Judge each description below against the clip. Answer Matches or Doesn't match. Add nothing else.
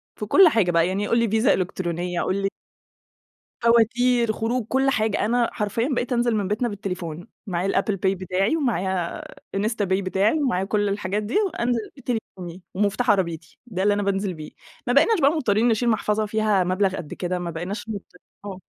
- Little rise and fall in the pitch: Doesn't match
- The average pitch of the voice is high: Matches